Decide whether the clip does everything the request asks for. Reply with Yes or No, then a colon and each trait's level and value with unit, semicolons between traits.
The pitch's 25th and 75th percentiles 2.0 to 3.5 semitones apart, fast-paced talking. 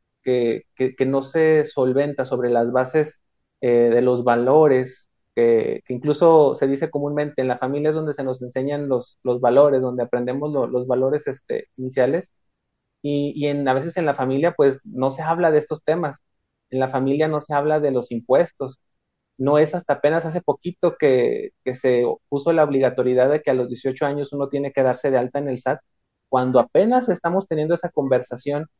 Yes: average, 3.1 semitones; fast, 195 wpm